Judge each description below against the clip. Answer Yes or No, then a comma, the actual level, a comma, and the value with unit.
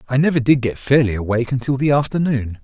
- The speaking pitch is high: No, low, 130 Hz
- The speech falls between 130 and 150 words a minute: No, fast, 205 wpm